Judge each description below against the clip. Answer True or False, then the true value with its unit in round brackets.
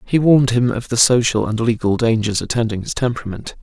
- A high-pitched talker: False (115 Hz)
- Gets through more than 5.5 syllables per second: True (6.0 syllables/s)